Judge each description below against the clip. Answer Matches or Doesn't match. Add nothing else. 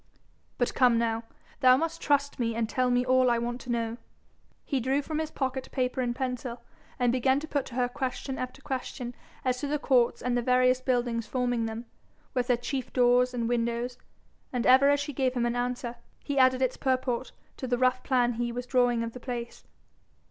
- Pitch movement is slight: Matches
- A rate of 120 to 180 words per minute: Doesn't match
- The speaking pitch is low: Doesn't match